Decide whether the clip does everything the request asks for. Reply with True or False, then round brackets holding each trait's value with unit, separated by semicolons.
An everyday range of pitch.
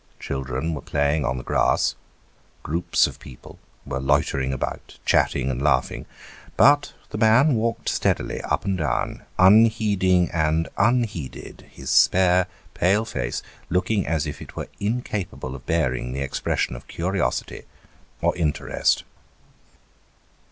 False (6.8 semitones)